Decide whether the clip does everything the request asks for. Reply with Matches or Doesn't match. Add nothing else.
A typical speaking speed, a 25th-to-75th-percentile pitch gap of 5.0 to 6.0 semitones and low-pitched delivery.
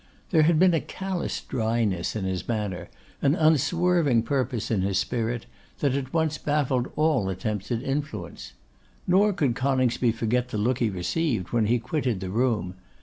Matches